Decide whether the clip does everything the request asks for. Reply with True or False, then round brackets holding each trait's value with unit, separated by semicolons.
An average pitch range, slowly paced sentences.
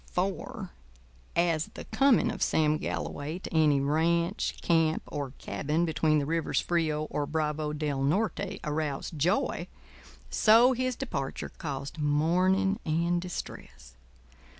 True (3.3 semitones; 125 wpm)